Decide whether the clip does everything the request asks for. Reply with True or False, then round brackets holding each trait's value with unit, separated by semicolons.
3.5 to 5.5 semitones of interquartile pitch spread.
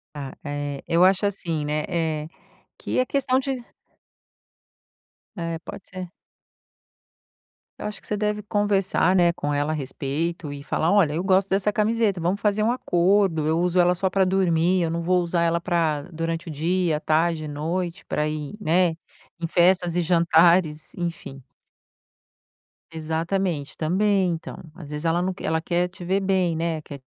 False (3.0 semitones)